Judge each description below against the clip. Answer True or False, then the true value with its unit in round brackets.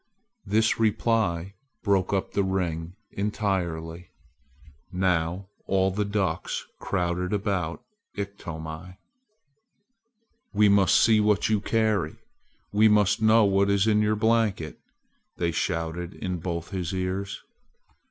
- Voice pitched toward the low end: True (95 Hz)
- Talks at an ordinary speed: False (115 wpm)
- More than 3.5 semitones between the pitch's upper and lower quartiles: False (3.1 semitones)